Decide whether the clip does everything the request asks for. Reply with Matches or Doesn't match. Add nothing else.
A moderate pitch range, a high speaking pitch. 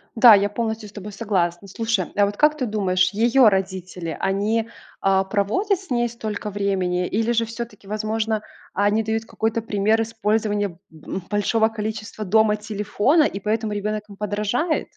Doesn't match